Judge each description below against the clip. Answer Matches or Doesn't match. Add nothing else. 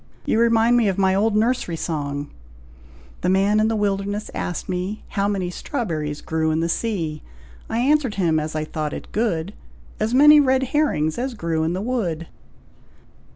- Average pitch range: Doesn't match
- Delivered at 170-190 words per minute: Matches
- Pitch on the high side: Matches